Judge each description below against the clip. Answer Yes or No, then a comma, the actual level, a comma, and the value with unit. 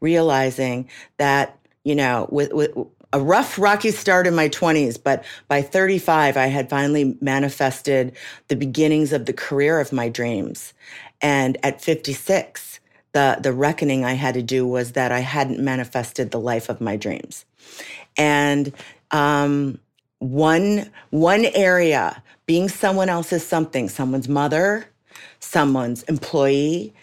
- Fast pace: No, slow, 135 wpm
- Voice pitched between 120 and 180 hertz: Yes, medium, 140 Hz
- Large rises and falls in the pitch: No, average, 3.3 semitones